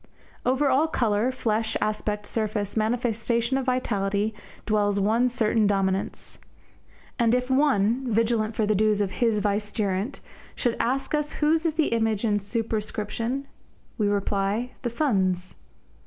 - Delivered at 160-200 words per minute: No, slow, 135 wpm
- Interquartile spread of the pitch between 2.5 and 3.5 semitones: Yes, average, 3.2 semitones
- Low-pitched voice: No, high, 220 Hz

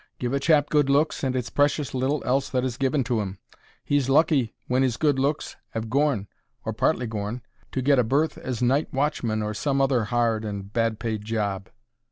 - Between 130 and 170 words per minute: No, average, 195 wpm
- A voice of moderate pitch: No, low, 125 Hz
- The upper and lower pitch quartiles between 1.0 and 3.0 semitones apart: No, average, 3.8 semitones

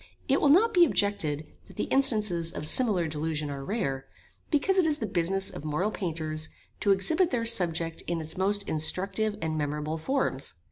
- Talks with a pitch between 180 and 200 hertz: Yes, medium, 185 Hz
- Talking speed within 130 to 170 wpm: No, average, 180 wpm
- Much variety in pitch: Yes, wide, 6.5 semitones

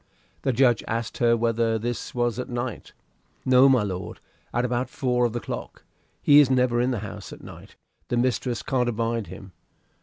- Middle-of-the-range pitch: No, low, 120 Hz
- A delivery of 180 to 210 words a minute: Yes, average, 185 wpm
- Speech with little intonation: Yes, narrow, 1.6 semitones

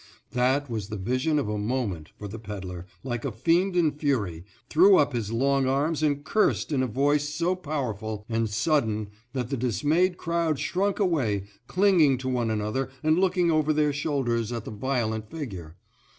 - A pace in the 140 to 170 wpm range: No, average, 180 wpm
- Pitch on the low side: Yes, low, 130 Hz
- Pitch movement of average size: No, wide, 5.9 semitones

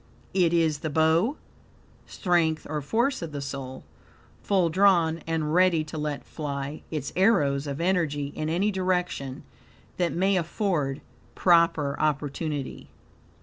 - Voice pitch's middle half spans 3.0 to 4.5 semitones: Yes, average, 3.5 semitones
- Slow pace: Yes, slow, 130 wpm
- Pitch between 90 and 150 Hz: No, medium, 160 Hz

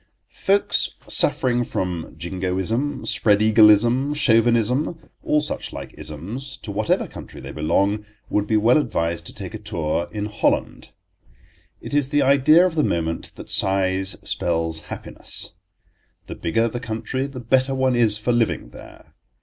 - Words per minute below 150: Yes, average, 140 wpm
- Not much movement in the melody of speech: No, wide, 5.6 semitones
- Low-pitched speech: Yes, low, 110 Hz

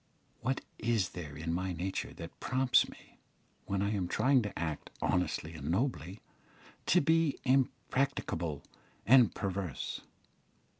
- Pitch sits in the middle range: No, low, 100 Hz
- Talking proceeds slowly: Yes, slow, 130 wpm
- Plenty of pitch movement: Yes, wide, 7.4 semitones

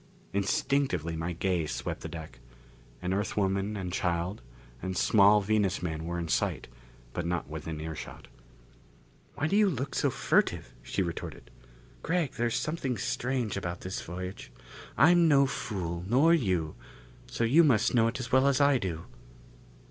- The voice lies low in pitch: Yes, low, 100 Hz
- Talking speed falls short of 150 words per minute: No, average, 160 wpm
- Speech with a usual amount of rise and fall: No, wide, 7.1 semitones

